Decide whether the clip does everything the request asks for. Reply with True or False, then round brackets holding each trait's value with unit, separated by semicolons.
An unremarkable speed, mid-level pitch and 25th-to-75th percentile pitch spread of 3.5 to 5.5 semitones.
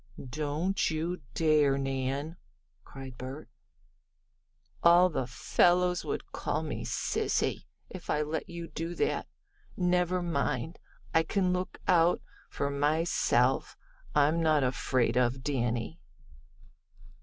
False (115 wpm; 155 Hz; 4.4 semitones)